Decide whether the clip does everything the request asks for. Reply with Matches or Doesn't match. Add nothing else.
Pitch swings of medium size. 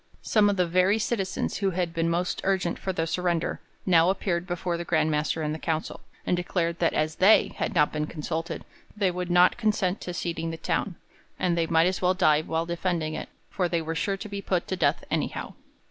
Doesn't match